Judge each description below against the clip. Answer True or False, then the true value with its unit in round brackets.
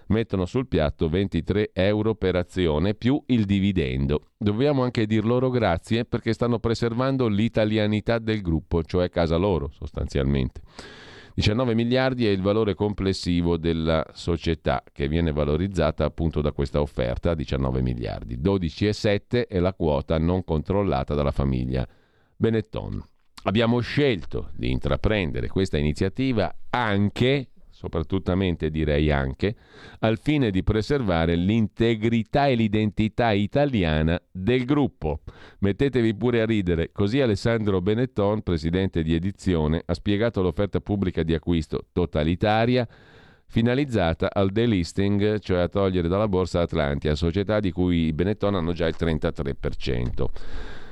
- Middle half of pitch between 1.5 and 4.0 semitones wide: False (5.2 semitones)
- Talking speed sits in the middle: True (125 wpm)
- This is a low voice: True (95 Hz)